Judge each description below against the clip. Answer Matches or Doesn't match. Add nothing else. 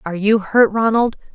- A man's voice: Doesn't match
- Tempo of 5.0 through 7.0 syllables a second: Matches